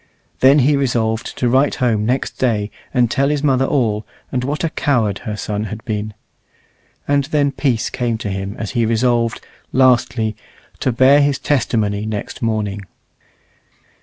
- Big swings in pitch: No, average, 3.7 semitones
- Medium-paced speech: Yes, average, 160 wpm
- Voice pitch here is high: No, low, 120 Hz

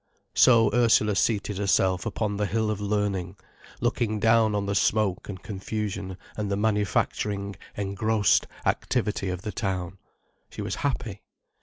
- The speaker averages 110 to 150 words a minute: Yes, average, 140 wpm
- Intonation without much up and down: Yes, narrow, 1.9 semitones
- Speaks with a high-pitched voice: No, low, 105 Hz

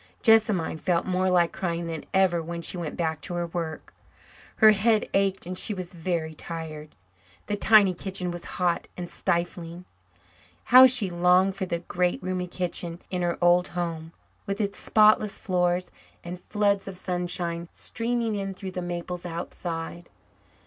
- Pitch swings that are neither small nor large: No, narrow, 2.2 semitones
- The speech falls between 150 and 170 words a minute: Yes, average, 160 wpm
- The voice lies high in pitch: No, medium, 180 Hz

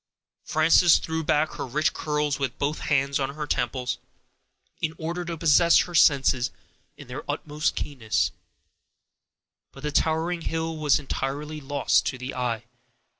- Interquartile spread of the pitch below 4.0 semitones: Yes, average, 2.8 semitones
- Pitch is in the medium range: Yes, medium, 150 Hz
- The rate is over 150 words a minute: No, average, 145 wpm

